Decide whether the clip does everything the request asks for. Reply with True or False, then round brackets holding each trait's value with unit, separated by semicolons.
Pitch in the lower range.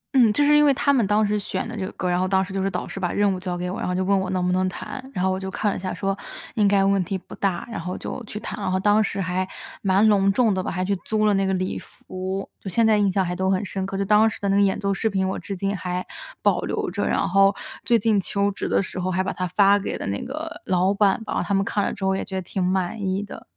False (195 Hz)